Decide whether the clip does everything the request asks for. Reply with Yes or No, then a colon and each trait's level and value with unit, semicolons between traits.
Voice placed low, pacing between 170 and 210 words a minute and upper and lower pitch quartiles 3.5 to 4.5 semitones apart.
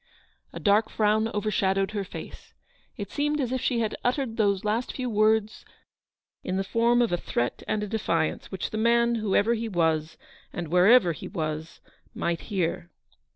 No: high, 210 Hz; average, 175 wpm; average, 4.2 semitones